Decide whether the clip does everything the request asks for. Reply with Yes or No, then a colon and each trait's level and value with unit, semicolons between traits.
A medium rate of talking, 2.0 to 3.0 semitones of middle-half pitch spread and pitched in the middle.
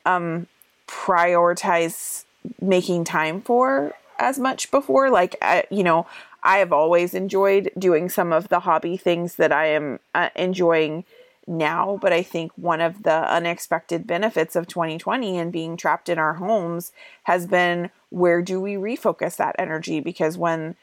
Yes: average, 155 wpm; narrow, 2.4 semitones; medium, 175 Hz